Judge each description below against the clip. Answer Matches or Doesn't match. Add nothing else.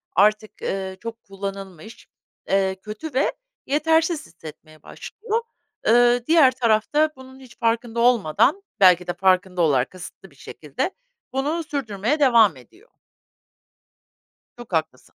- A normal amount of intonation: Doesn't match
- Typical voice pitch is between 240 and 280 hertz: Doesn't match